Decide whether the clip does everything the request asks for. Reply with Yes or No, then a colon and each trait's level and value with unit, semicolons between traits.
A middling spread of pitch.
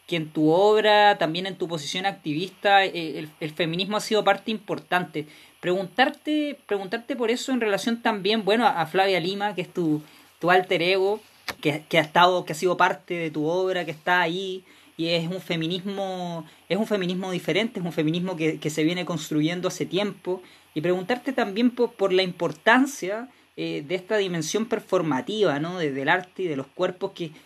Yes: average, 3.7 semitones